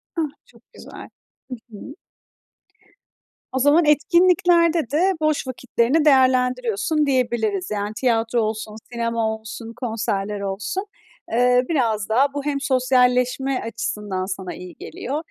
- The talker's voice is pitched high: Yes, very high, 250 Hz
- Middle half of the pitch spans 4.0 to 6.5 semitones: Yes, average, 4.6 semitones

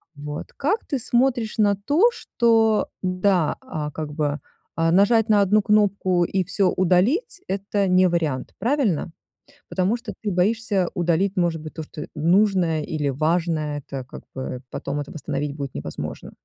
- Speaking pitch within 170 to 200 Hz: Yes, medium, 185 Hz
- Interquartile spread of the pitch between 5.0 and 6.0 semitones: Yes, wide, 5.4 semitones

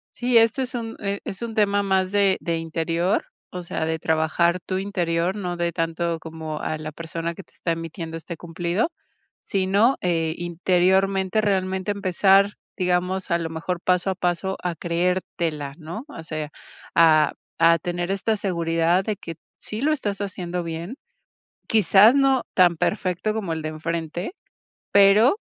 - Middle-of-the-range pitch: Yes, medium, 180 Hz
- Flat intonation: No, average, 3.1 semitones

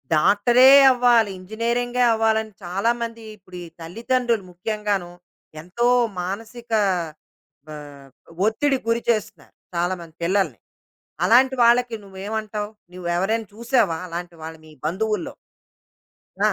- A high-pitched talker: Yes, high, 215 Hz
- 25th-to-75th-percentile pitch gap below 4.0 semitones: No, average, 4.7 semitones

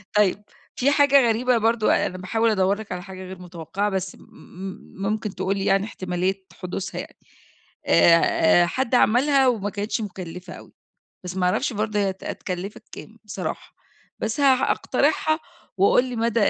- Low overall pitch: No, high, 200 Hz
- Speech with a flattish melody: No, average, 3.7 semitones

